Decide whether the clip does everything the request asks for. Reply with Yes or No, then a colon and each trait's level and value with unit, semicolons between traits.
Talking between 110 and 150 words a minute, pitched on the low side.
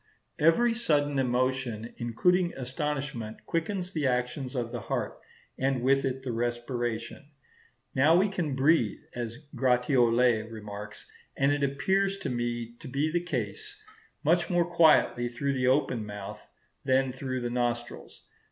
Yes: average, 140 wpm; low, 130 Hz